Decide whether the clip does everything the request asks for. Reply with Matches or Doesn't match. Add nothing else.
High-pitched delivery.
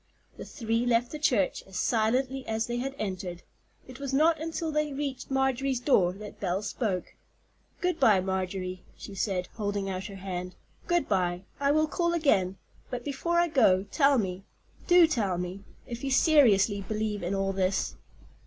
Matches